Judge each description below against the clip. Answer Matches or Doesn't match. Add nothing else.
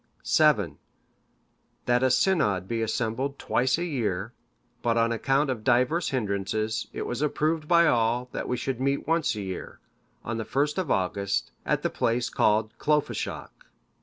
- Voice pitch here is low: Matches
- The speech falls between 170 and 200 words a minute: Doesn't match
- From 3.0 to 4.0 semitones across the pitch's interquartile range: Doesn't match